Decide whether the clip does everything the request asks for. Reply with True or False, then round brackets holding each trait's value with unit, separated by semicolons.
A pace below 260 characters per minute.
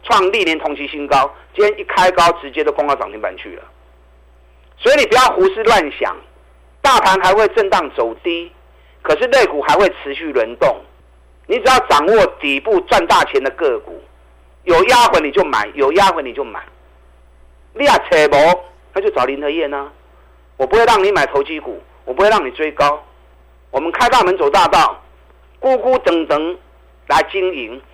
True (250 characters per minute)